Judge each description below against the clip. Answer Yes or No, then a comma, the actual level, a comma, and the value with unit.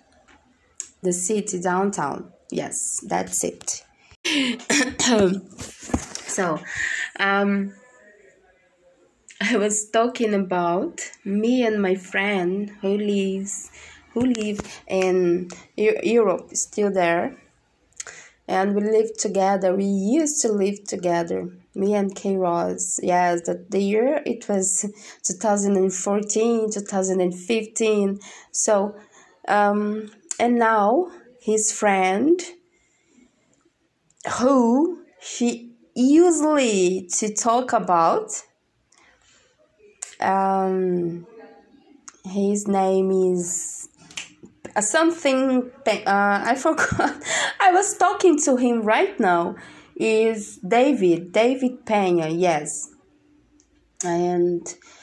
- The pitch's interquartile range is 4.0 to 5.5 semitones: Yes, average, 4.6 semitones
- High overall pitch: Yes, high, 210 Hz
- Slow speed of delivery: Yes, slow, 85 wpm